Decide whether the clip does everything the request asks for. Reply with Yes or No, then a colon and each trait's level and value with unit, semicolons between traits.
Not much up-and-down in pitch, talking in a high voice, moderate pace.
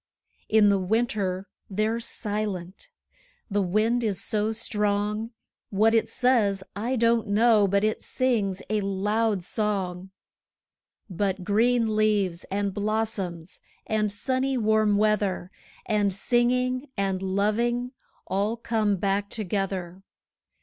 No: narrow, 2.3 semitones; high, 210 Hz; slow, 115 wpm